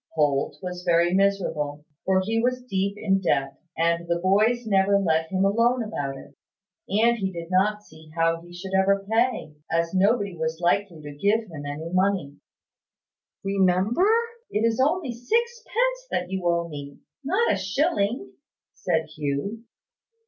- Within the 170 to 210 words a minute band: No, average, 155 wpm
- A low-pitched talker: No, high, 190 Hz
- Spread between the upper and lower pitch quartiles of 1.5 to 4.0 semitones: No, average, 4.9 semitones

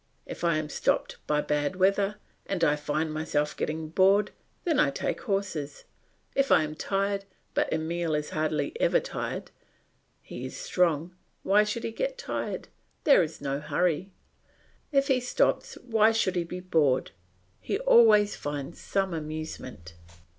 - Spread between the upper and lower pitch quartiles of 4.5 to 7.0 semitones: Yes, average, 5.3 semitones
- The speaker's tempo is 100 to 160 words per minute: Yes, average, 155 wpm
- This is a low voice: No, medium, 175 Hz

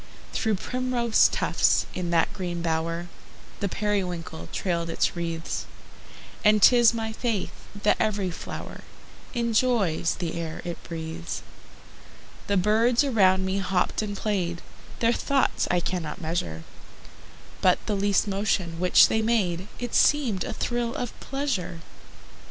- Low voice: No, high, 195 Hz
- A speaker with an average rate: No, slow, 130 wpm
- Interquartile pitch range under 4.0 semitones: No, average, 4.6 semitones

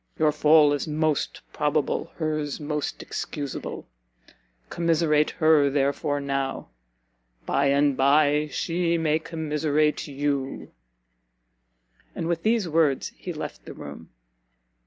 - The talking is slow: Yes, slow, 110 wpm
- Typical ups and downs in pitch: No, narrow, 1.9 semitones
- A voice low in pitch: No, medium, 150 Hz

